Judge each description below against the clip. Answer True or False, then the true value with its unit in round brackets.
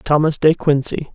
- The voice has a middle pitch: True (150 Hz)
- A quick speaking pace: False (155 wpm)